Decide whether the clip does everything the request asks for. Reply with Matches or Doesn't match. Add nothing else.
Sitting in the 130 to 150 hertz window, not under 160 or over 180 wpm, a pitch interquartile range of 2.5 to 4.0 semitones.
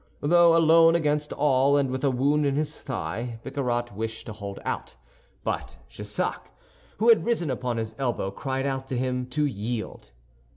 Matches